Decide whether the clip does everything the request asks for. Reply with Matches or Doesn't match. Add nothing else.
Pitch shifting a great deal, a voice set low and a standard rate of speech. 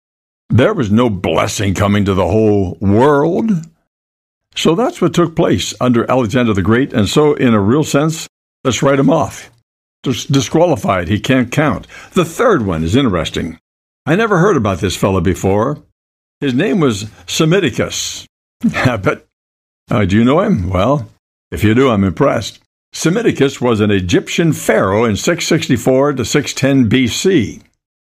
Matches